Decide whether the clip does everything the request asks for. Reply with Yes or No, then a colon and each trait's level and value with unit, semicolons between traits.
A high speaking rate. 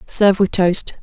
No: average, 175 wpm